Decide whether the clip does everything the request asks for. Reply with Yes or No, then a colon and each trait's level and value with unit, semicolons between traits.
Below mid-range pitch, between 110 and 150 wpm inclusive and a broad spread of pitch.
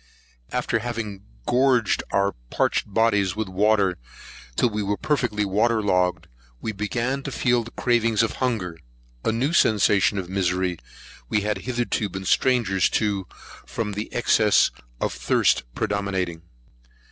No: low, 105 Hz; slow, 135 wpm; average, 3.4 semitones